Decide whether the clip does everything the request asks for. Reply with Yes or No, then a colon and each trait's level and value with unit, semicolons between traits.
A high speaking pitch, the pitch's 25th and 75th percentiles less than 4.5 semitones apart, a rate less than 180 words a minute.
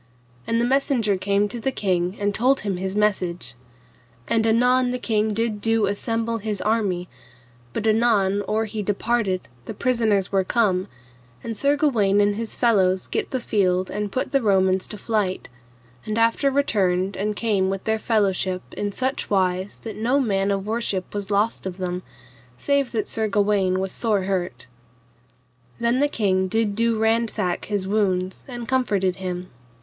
Yes: high, 210 Hz; average, 3.2 semitones; average, 165 wpm